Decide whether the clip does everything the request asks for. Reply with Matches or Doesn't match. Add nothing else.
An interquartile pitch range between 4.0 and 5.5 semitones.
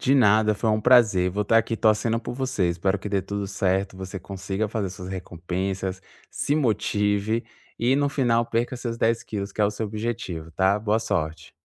Doesn't match